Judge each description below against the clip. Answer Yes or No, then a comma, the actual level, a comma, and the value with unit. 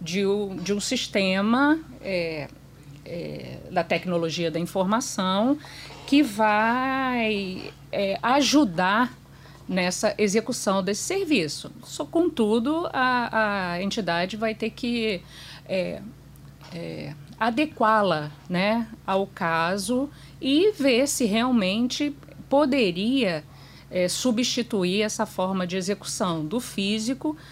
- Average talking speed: No, slow, 100 wpm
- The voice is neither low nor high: No, high, 215 Hz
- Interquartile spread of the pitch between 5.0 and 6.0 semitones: Yes, wide, 5.5 semitones